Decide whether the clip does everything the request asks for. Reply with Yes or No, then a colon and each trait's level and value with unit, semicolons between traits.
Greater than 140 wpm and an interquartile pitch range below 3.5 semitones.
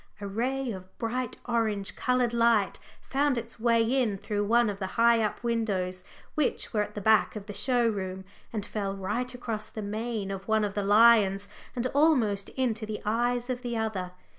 Yes: average, 190 wpm; average, 2.9 semitones